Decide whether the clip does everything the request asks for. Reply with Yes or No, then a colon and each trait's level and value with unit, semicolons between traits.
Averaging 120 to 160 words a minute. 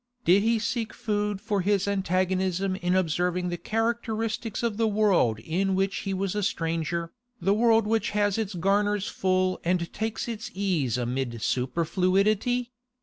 Yes: average, 150 wpm